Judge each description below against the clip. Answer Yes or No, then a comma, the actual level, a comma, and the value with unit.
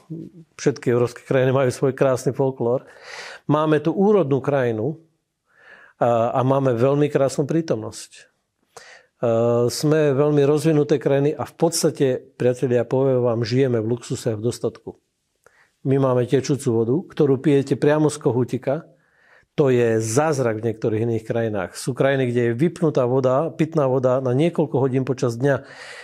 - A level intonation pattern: No, average, 3.8 semitones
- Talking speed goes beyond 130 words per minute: Yes, average, 145 wpm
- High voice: No, low, 135 Hz